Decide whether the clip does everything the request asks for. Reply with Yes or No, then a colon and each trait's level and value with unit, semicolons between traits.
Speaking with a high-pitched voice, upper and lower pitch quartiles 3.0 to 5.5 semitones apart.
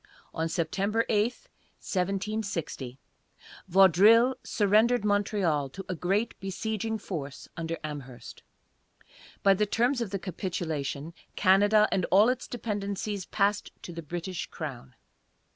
Yes: high, 195 Hz; average, 4.1 semitones